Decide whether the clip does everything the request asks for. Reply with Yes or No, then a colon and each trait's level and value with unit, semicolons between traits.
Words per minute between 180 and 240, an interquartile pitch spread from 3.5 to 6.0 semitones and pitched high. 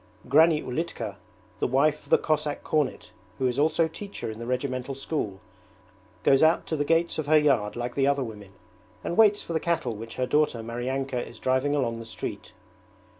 No: average, 190 wpm; average, 4.2 semitones; low, 135 Hz